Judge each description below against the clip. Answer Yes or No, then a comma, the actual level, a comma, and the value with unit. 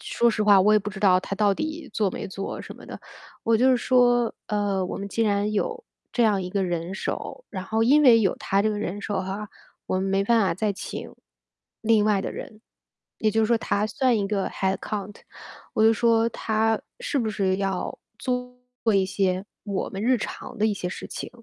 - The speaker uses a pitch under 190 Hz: No, high, 210 Hz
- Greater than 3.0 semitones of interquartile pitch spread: No, average, 2.7 semitones